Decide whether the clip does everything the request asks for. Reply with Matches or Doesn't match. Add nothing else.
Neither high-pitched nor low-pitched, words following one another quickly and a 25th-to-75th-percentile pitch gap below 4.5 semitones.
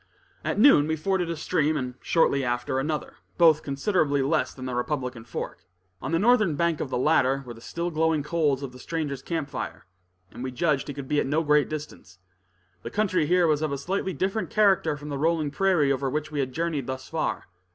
Matches